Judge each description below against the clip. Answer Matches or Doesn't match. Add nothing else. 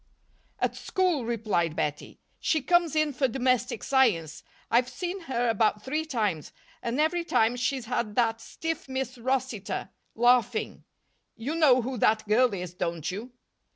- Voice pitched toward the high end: Matches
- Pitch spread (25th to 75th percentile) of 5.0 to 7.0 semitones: Doesn't match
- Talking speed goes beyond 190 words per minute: Doesn't match